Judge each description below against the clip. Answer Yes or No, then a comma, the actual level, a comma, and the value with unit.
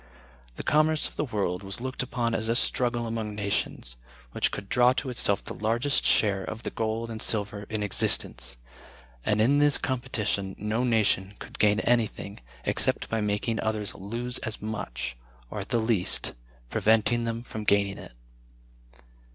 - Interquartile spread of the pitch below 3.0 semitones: Yes, narrow, 2.6 semitones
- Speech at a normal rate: Yes, average, 165 wpm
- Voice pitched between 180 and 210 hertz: No, low, 110 Hz